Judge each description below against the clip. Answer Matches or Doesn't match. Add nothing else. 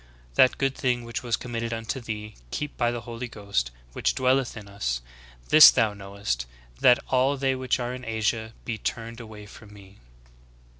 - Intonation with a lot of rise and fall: Doesn't match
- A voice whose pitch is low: Matches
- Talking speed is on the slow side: Doesn't match